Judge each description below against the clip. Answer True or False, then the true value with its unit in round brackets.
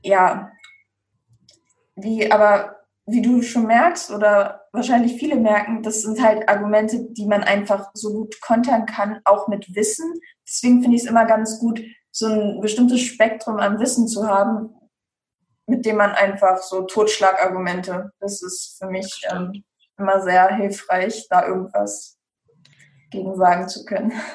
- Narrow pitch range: False (3.0 semitones)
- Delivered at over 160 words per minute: False (150 wpm)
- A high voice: True (210 Hz)